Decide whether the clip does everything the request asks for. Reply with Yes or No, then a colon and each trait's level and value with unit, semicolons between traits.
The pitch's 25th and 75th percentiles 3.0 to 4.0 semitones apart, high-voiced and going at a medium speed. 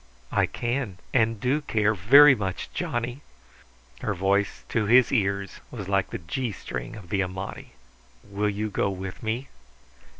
No: average, 3.5 semitones; low, 105 Hz; average, 155 wpm